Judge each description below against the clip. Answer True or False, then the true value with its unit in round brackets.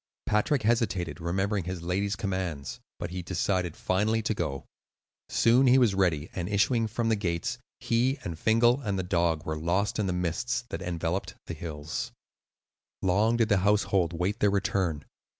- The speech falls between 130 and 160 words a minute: False (170 wpm)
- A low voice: True (95 Hz)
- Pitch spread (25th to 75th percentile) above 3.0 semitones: True (4.2 semitones)